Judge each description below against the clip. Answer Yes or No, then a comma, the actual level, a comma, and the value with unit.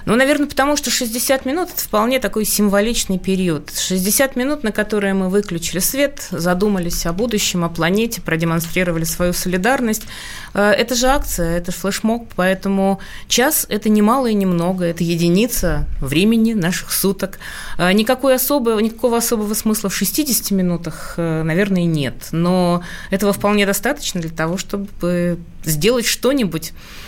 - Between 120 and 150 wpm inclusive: Yes, average, 140 wpm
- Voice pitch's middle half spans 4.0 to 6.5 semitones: Yes, average, 4.8 semitones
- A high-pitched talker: Yes, high, 200 Hz